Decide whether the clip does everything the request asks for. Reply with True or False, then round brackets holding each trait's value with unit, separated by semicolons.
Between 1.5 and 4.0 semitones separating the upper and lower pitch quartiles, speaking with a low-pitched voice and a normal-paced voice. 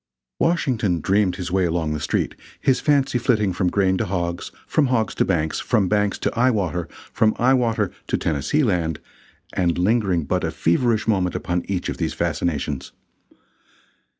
False (4.8 semitones; 95 Hz; 170 wpm)